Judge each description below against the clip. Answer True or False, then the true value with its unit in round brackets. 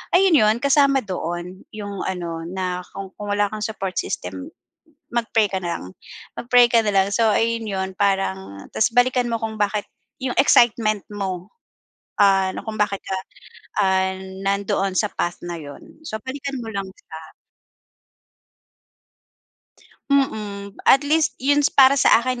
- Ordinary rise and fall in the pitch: True (3.9 semitones)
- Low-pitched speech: False (205 Hz)